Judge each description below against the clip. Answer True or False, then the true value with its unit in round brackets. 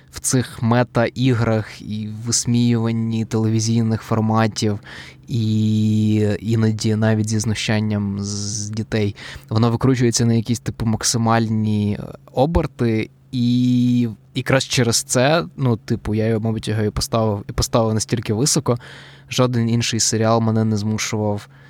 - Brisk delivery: False (125 wpm)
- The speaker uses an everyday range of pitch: False (2.1 semitones)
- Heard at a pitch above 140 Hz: False (115 Hz)